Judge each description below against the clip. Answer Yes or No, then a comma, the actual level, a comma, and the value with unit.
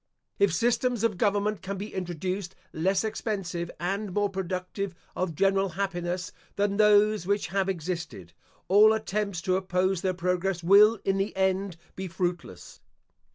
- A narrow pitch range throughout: Yes, narrow, 2.1 semitones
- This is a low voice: No, high, 190 Hz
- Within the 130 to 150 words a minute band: Yes, average, 145 wpm